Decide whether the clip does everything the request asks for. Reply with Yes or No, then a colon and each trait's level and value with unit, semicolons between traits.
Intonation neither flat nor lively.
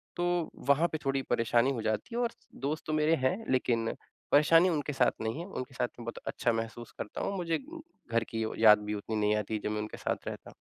No: wide, 6.1 semitones